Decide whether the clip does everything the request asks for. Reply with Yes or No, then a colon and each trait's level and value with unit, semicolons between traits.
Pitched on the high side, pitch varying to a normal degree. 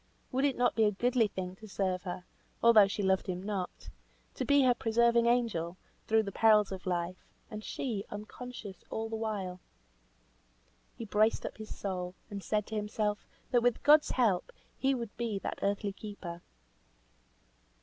Yes: high, 210 Hz; average, 3.4 semitones